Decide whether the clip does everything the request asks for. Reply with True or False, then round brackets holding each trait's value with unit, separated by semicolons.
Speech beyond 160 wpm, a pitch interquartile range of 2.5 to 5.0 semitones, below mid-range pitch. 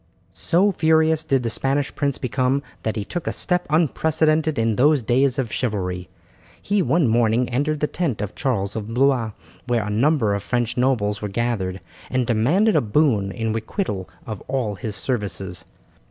False (170 wpm; 5.6 semitones; 125 Hz)